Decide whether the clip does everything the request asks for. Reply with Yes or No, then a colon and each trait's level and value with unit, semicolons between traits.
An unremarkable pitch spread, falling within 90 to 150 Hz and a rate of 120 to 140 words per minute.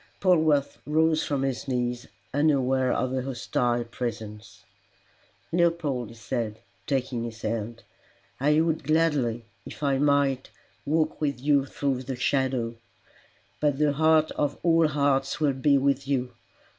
Yes: average, 3.3 semitones; low, 135 Hz; slow, 135 wpm